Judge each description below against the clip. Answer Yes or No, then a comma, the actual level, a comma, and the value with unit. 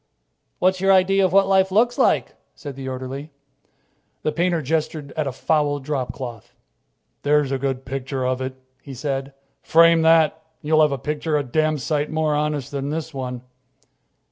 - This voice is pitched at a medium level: Yes, medium, 150 Hz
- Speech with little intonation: No, average, 3.2 semitones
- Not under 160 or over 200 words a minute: Yes, average, 170 wpm